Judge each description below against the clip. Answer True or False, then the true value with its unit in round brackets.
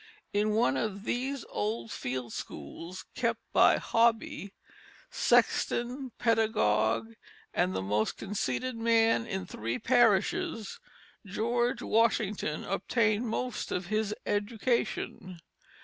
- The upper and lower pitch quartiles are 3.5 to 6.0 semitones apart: True (4.6 semitones)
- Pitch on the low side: False (215 Hz)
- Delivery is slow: True (100 wpm)